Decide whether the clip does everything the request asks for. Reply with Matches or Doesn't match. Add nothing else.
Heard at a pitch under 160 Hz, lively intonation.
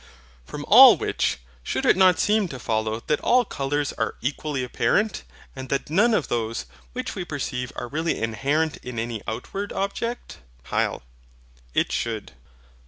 Matches